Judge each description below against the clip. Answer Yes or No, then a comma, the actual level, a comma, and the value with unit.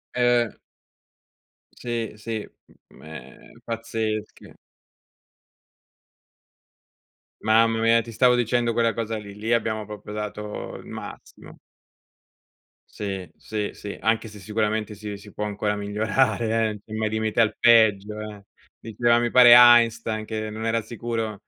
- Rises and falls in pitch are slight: Yes, narrow, 1.5 semitones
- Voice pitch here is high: No, low, 110 Hz